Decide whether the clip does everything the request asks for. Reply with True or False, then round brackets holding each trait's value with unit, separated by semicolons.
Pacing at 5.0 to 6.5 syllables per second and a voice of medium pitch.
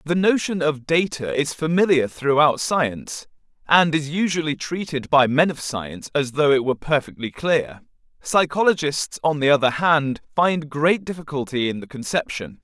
False (4.8 syllables/s; 150 Hz)